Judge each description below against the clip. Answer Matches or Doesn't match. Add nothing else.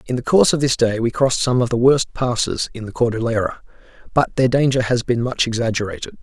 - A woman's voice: Doesn't match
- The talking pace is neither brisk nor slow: Doesn't match